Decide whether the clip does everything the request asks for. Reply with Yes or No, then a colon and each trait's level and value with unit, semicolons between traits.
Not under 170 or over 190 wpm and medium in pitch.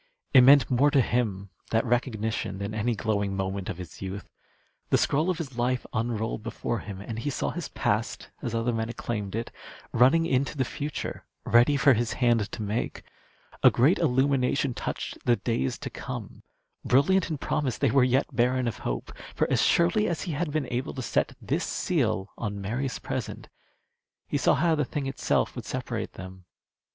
No: average, 185 wpm; low, 120 Hz